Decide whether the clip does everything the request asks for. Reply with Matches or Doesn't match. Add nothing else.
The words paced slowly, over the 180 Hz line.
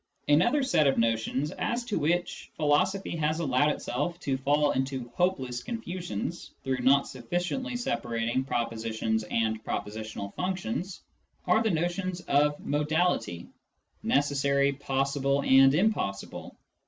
Doesn't match